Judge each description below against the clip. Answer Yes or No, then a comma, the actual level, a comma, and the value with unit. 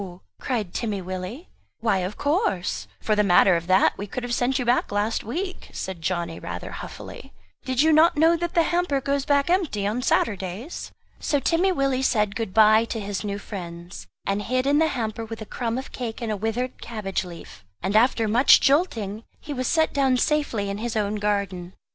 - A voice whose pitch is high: Yes, high, 225 Hz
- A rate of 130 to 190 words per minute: No, average, 200 wpm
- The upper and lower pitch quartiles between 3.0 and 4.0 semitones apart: No, wide, 5.5 semitones